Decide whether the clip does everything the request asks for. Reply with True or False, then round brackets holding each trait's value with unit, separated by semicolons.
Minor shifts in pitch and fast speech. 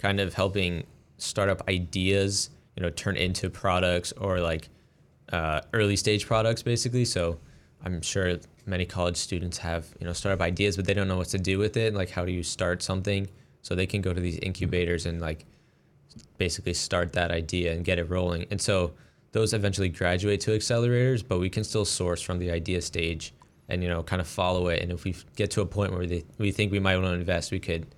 True (2.3 semitones; 215 wpm)